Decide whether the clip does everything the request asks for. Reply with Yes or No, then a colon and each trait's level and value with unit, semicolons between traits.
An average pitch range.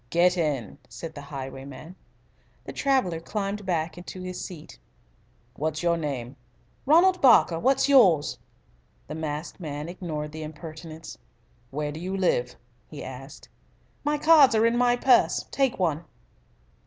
No: wide, 5.7 semitones